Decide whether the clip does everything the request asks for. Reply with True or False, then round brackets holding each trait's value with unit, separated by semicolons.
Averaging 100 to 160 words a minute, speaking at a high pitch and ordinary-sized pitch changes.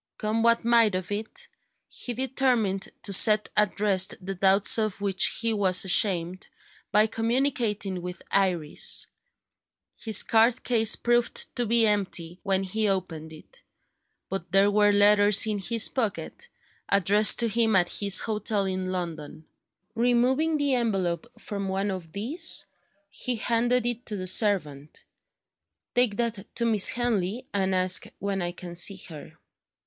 True (145 wpm; 205 Hz; 3.6 semitones)